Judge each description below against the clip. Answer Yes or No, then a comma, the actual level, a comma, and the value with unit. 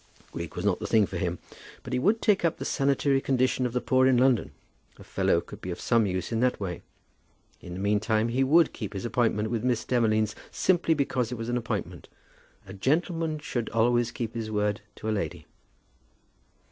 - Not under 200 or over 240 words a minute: Yes, fast, 205 wpm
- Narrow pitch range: No, average, 3.7 semitones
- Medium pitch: No, low, 120 Hz